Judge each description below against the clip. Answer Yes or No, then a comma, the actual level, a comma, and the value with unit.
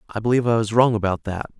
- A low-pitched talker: Yes, low, 110 Hz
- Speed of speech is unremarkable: No, fast, 265 wpm